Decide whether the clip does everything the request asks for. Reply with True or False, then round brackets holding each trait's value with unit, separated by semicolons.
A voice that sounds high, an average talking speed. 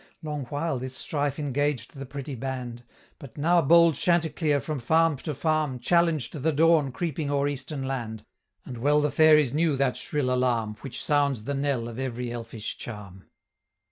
False (140 Hz; 170 wpm)